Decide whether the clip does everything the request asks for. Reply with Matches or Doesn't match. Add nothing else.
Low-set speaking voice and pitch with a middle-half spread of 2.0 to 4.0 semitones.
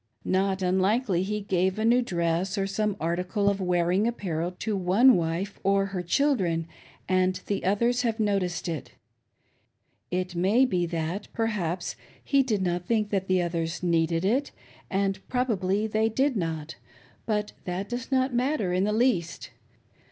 Doesn't match